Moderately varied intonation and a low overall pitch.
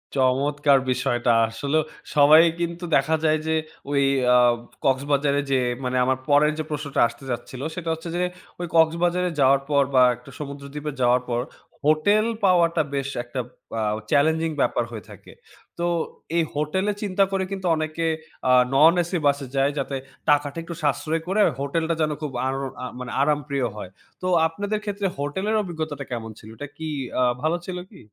No: average, 3.4 semitones; medium, 145 Hz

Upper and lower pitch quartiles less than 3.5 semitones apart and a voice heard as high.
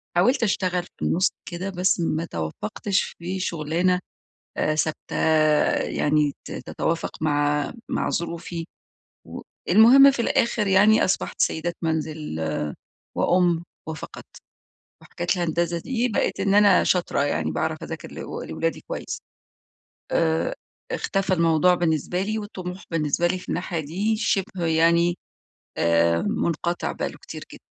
No: average, 3.0 semitones; medium, 175 Hz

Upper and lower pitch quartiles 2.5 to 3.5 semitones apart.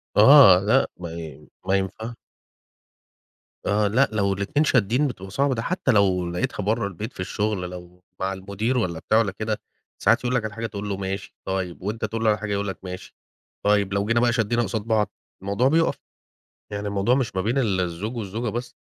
Yes: average, 3.2 semitones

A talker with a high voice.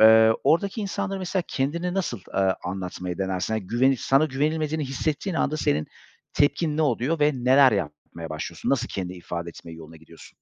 No: low, 125 Hz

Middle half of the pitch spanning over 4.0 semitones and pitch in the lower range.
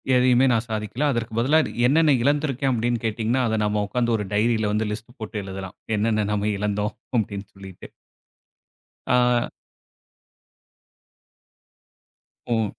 No: average, 2.9 semitones; low, 110 Hz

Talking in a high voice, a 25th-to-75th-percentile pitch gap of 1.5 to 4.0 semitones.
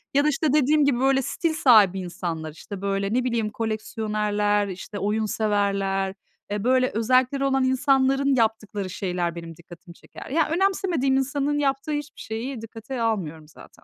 No: high, 225 Hz; wide, 5.4 semitones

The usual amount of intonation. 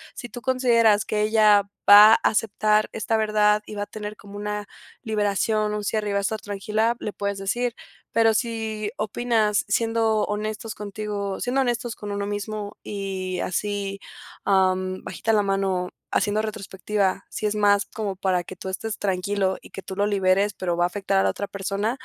No: narrow, 1.5 semitones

